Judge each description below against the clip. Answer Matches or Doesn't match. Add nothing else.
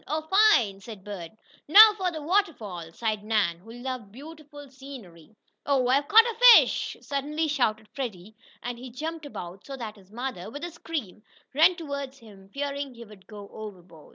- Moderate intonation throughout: Doesn't match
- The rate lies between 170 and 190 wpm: Matches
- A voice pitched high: Matches